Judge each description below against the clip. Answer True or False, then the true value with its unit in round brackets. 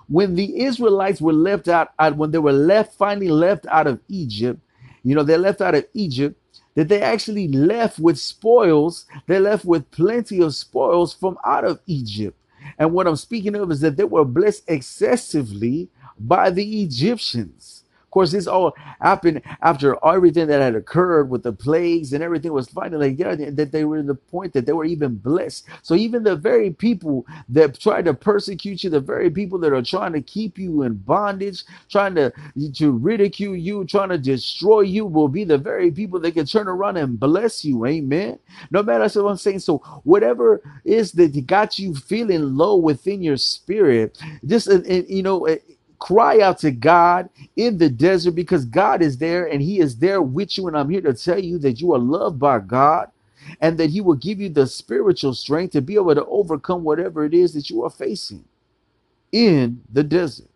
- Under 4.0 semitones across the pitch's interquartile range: False (5.1 semitones)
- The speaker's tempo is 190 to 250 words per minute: True (200 wpm)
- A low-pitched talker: False (170 Hz)